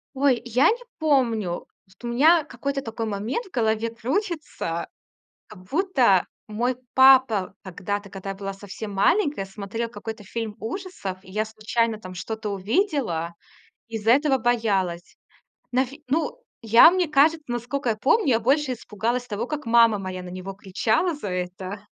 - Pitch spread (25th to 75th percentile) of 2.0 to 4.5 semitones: No, average, 5.3 semitones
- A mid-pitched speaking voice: No, high, 225 Hz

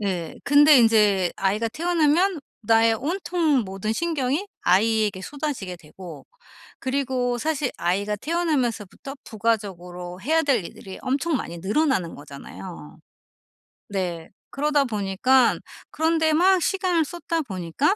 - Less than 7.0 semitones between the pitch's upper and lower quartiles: No, wide, 8.0 semitones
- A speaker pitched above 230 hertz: Yes, high, 240 Hz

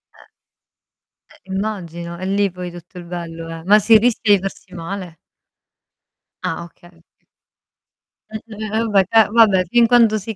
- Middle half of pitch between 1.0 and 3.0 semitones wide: No, average, 4.0 semitones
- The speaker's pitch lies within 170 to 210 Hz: Yes, high, 190 Hz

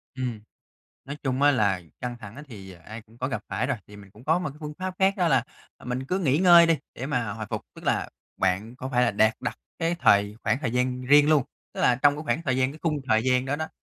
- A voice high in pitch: No, low, 130 Hz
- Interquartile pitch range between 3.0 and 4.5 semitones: No, average, 5.0 semitones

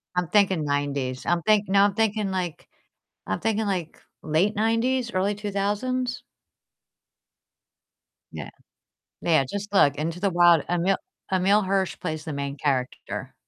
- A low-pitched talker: No, high, 190 Hz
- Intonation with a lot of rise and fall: No, average, 4.7 semitones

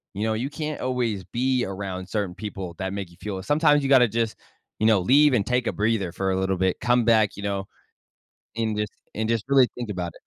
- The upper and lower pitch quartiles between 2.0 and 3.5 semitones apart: No, average, 4.3 semitones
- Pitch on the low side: Yes, low, 110 Hz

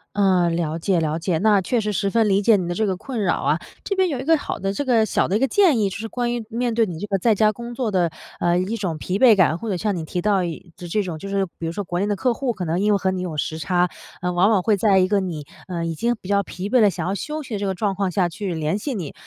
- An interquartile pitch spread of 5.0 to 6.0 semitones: No, average, 3.8 semitones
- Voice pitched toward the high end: Yes, high, 195 Hz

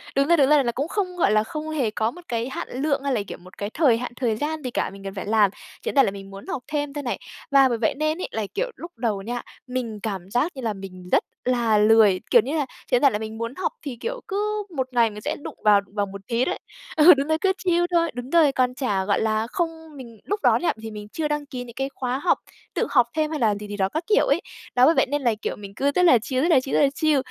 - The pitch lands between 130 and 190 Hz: No, very high, 255 Hz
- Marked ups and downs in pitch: Yes, wide, 5.7 semitones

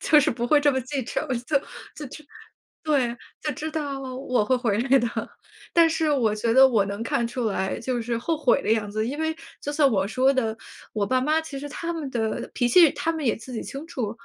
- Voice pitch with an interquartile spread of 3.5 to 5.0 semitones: Yes, average, 4.3 semitones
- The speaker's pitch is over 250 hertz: Yes, very high, 260 Hz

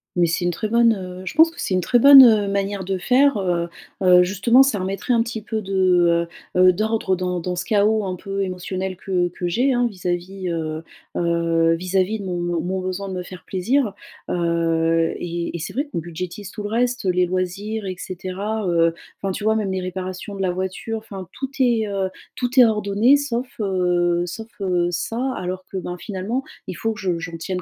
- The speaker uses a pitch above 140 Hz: Yes, high, 190 Hz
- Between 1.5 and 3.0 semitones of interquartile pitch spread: No, average, 3.5 semitones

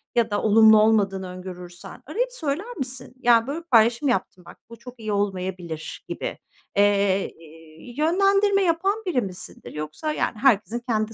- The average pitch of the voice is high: Yes, high, 225 Hz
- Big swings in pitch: Yes, wide, 6.8 semitones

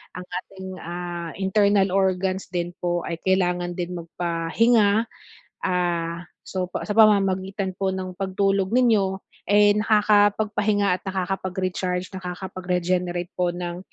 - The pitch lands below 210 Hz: Yes, medium, 185 Hz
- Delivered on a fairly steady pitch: Yes, narrow, 1.8 semitones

